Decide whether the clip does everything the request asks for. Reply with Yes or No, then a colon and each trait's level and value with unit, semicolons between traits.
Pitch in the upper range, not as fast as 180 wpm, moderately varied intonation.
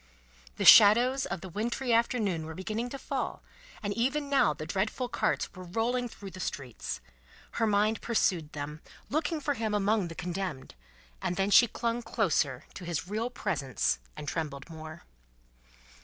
No: high, 200 Hz; average, 160 wpm; wide, 6.2 semitones